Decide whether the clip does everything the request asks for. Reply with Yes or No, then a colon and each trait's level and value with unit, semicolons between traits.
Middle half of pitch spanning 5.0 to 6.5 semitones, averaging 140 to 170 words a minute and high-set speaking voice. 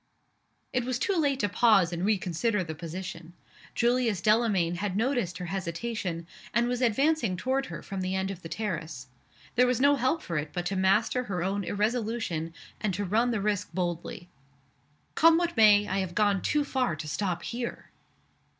No: average, 5.3 semitones; average, 180 wpm; high, 205 Hz